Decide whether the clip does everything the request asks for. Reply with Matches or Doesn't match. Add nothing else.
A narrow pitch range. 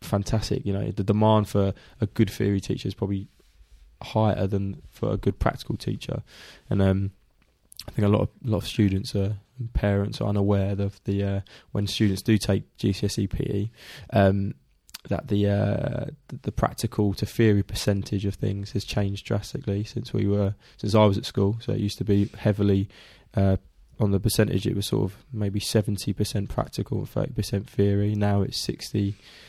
Matches